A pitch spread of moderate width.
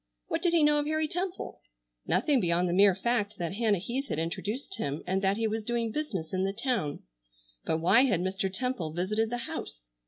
No: wide, 5.8 semitones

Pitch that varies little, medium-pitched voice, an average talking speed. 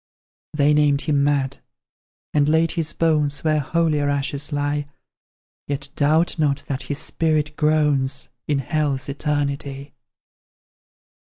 No: narrow, 1.4 semitones; medium, 145 Hz; slow, 115 wpm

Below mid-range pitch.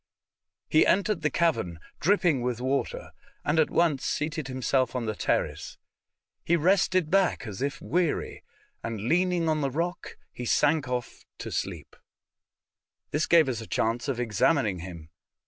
No: medium, 145 Hz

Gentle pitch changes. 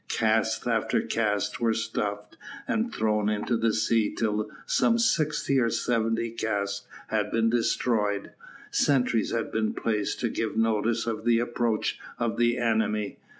Yes: narrow, 1.7 semitones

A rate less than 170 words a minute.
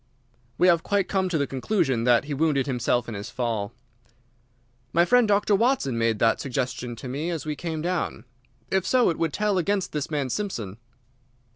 No: average, 185 wpm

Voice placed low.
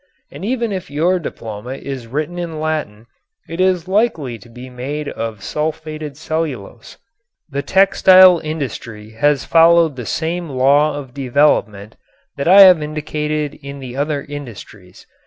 No: medium, 150 Hz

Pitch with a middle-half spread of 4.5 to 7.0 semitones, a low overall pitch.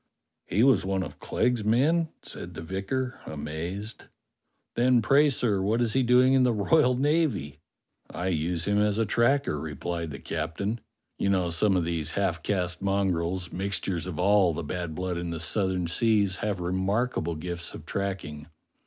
Yes: average, 5.1 semitones; very low, 95 Hz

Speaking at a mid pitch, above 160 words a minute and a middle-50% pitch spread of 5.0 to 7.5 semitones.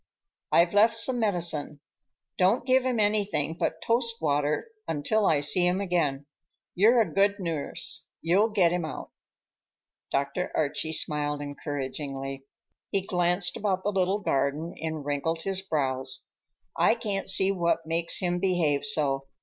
No: medium, 175 Hz; average, 140 wpm; average, 5.3 semitones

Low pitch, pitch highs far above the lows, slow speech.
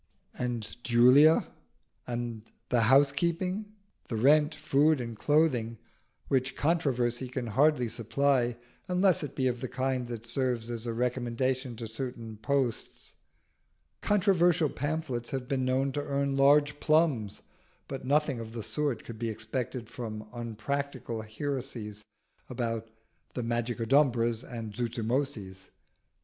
No: low, 125 Hz; average, 3.4 semitones; slow, 125 wpm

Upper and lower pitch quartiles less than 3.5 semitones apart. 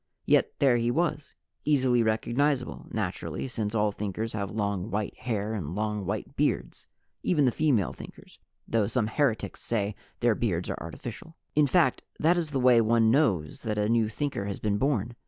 No: average, 4.2 semitones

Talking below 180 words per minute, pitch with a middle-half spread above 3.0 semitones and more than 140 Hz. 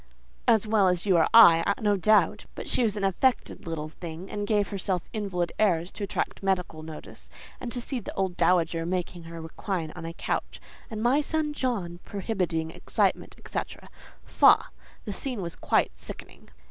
Yes: average, 170 wpm; average, 4.3 semitones; high, 190 Hz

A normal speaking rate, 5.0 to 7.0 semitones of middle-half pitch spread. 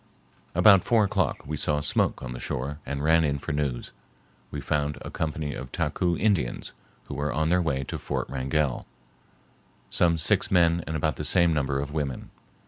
No: average, 185 wpm; average, 3.1 semitones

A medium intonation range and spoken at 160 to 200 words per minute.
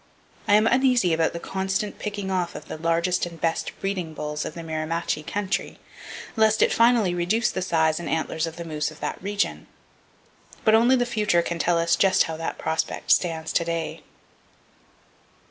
Yes: average, 3.9 semitones; average, 180 wpm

